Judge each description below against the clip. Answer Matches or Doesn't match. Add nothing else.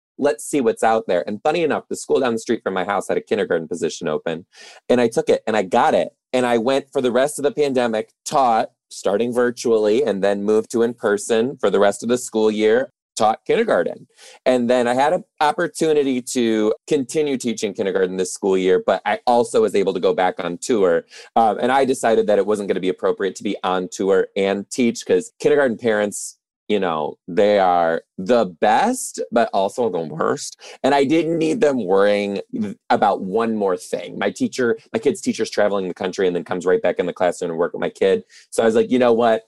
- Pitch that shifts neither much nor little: Doesn't match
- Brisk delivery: Matches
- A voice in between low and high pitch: Doesn't match